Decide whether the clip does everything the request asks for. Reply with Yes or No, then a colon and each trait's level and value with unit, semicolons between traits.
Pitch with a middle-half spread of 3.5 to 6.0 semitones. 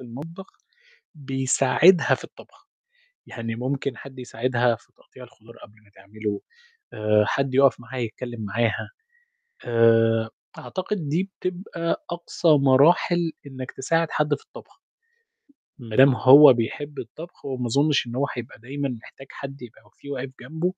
Yes: average, 4.0 semitones